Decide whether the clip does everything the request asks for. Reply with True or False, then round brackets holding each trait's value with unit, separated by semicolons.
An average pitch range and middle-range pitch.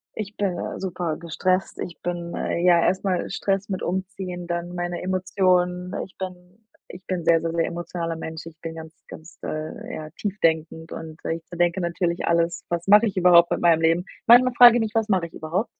False (2.1 semitones; 175 Hz)